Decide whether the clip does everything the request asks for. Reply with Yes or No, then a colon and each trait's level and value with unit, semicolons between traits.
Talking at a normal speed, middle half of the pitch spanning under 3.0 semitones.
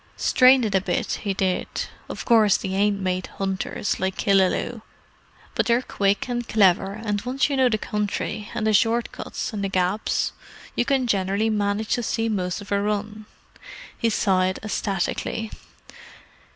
Yes: average, 165 wpm; narrow, 2.6 semitones